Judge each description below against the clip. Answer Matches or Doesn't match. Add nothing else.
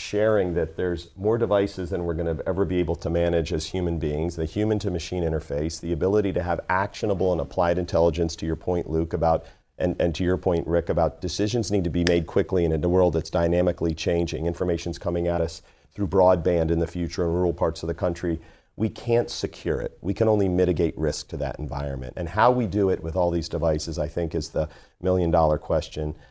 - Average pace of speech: Doesn't match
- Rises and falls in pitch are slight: Matches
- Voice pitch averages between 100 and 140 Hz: Doesn't match